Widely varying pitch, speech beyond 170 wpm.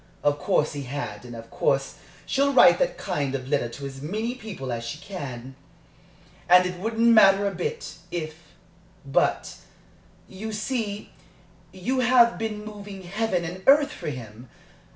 No: wide, 8.1 semitones; average, 155 wpm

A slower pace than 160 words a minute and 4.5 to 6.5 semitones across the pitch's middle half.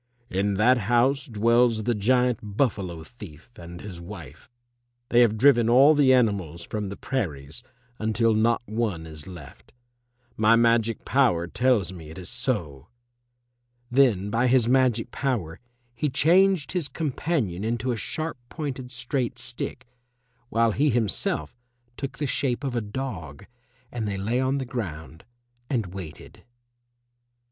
Yes: average, 140 wpm; average, 5.0 semitones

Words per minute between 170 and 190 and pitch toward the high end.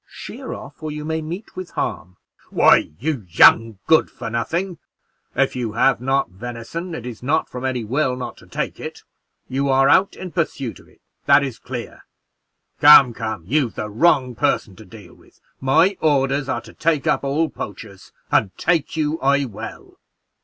No: average, 180 wpm; low, 135 Hz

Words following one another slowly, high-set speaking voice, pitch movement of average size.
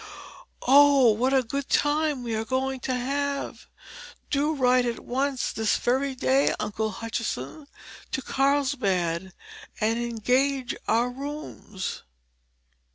Yes: slow, 115 wpm; very high, 255 Hz; average, 3.6 semitones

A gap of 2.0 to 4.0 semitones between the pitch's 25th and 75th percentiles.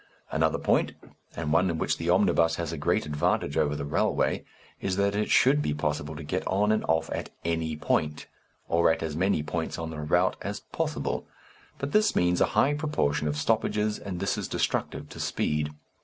No: average, 4.9 semitones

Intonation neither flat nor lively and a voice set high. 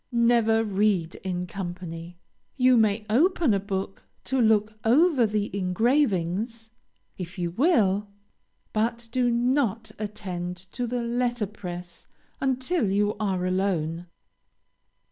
Yes: average, 4.5 semitones; high, 210 Hz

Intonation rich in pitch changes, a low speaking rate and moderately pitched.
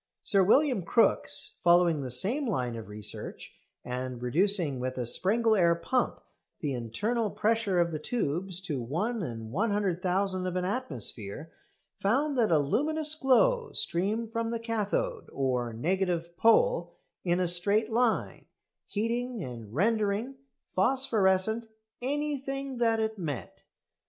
No: wide, 6.3 semitones; slow, 125 wpm; high, 195 Hz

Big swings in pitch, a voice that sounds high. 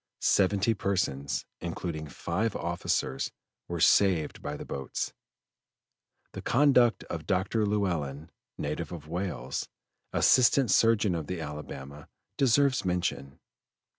No: wide, 5.7 semitones; very low, 90 Hz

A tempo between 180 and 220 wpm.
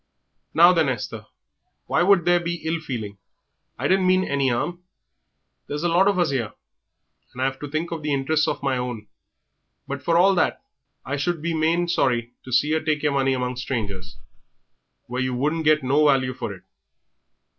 Yes: average, 190 wpm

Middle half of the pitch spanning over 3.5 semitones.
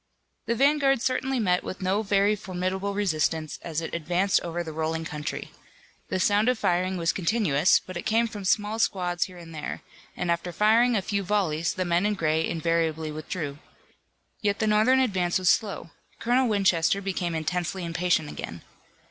Yes: average, 3.9 semitones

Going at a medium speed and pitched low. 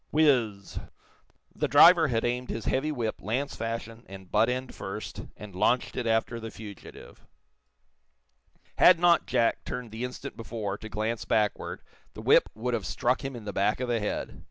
Yes: average, 180 wpm; low, 115 Hz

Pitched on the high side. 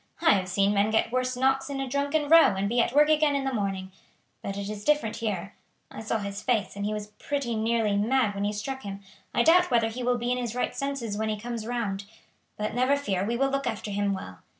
Yes: high, 230 Hz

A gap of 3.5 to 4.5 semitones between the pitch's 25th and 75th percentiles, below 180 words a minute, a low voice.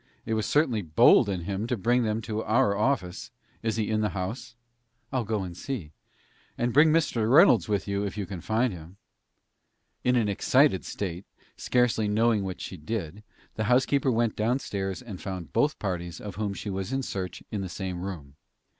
No: average, 4.0 semitones; average, 190 wpm; low, 105 Hz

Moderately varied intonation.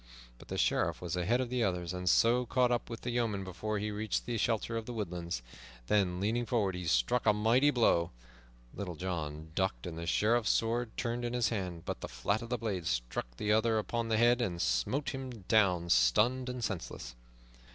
Yes: average, 5.0 semitones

